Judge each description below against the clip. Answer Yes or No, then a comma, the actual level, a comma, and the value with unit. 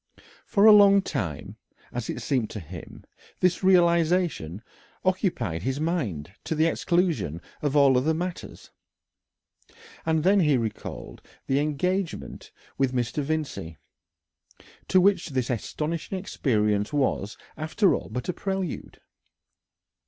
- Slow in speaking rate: Yes, slow, 125 wpm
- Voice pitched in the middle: Yes, medium, 155 Hz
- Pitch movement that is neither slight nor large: No, wide, 6.9 semitones